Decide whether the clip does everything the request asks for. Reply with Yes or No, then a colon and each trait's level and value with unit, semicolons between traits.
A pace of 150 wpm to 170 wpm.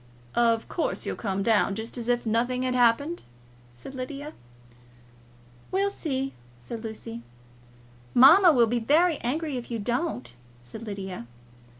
No: slow, 135 wpm